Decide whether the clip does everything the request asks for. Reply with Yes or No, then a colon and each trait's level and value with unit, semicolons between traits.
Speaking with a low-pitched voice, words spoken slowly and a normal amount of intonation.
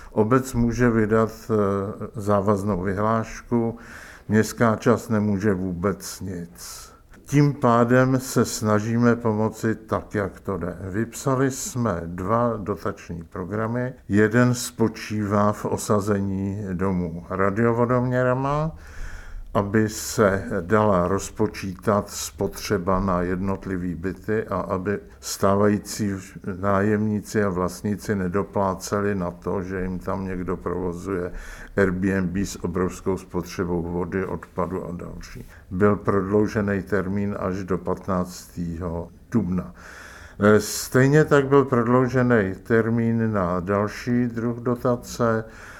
Yes: low, 100 Hz; slow, 100 wpm; average, 3.4 semitones